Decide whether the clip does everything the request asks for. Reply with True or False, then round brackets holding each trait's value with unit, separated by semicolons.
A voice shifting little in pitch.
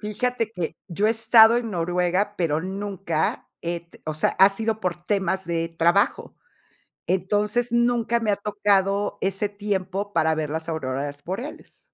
False (3.8 semitones)